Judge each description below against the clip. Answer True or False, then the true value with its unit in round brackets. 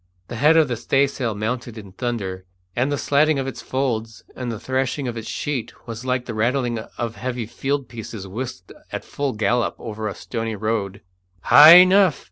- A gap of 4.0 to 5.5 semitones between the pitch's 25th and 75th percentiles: False (3.4 semitones)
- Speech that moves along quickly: False (185 wpm)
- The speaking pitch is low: True (120 Hz)